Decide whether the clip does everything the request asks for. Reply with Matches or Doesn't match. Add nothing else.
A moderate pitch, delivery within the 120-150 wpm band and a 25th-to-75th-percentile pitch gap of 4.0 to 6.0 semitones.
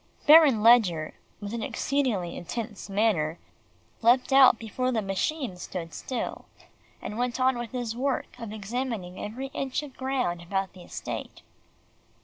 Doesn't match